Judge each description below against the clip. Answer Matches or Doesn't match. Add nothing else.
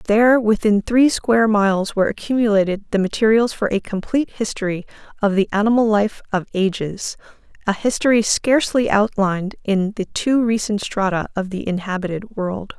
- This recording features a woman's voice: Matches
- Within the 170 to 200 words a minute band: Doesn't match